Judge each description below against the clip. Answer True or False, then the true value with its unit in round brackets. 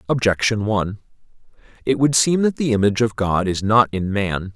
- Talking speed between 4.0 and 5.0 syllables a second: False (5.5 syllables/s)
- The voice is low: True (110 Hz)